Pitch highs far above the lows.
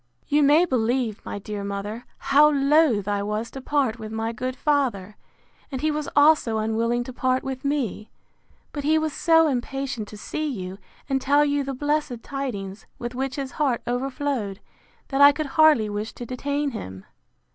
No: average, 4.6 semitones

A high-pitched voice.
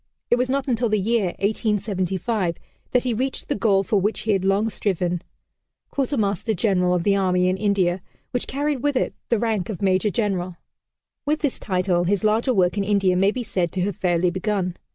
Yes: high, 200 Hz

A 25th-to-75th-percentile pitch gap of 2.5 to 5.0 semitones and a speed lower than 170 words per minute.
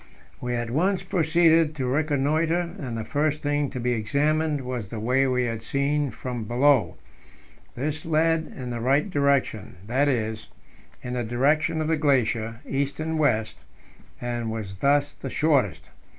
Yes: average, 4.3 semitones; average, 160 wpm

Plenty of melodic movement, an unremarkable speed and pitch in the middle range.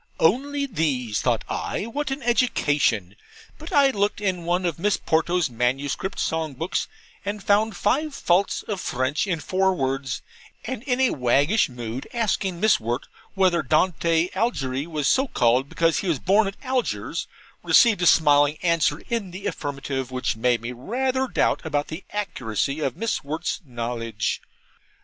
Yes: wide, 7.4 semitones; average, 160 wpm; medium, 170 Hz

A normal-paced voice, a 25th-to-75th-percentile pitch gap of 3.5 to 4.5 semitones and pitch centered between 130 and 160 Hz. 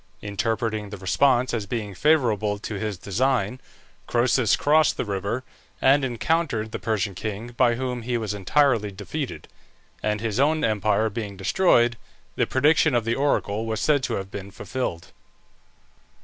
No: average, 150 wpm; average, 4.0 semitones; low, 115 Hz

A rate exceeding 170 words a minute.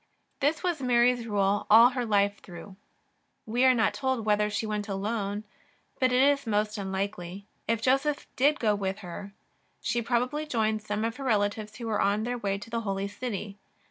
Yes: average, 190 wpm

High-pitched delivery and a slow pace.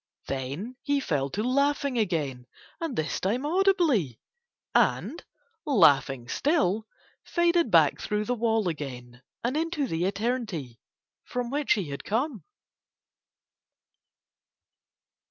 Yes: high, 220 Hz; slow, 110 wpm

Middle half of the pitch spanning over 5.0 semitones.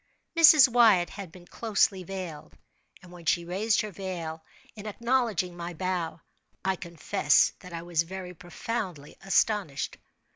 No: average, 3.5 semitones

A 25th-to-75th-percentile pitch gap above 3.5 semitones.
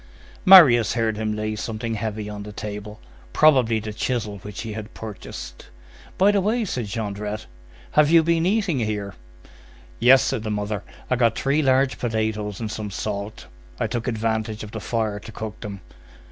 No: average, 3.1 semitones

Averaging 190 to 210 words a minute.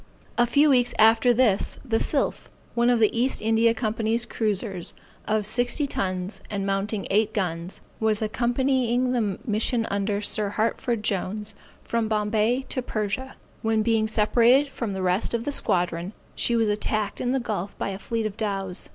No: average, 170 wpm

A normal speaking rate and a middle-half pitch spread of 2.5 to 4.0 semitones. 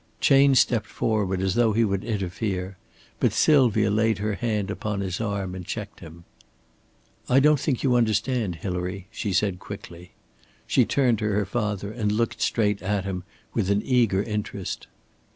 Yes: average, 165 wpm; average, 3.1 semitones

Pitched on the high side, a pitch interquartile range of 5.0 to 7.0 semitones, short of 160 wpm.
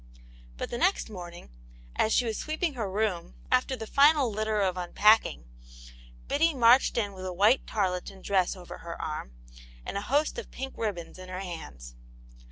No: high, 210 Hz; wide, 5.6 semitones; average, 175 wpm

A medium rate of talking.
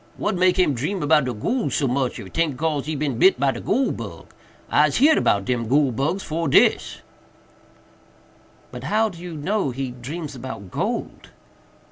Yes: average, 175 wpm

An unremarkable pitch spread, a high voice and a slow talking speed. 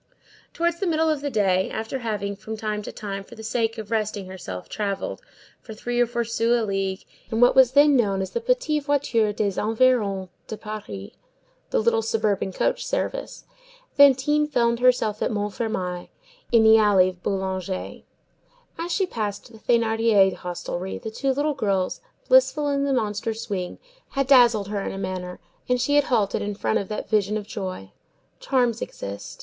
No: average, 4.2 semitones; high, 220 Hz; average, 175 wpm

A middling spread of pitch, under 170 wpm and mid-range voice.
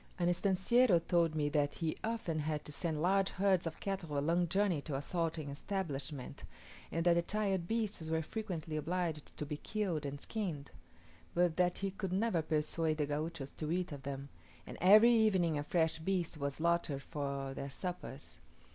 No: average, 3.9 semitones; average, 180 wpm; medium, 165 Hz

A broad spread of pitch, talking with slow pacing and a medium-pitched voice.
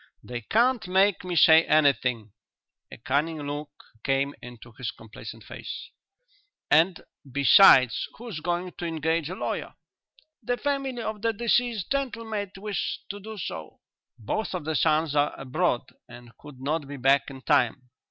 No: wide, 7.1 semitones; average, 150 wpm; medium, 160 Hz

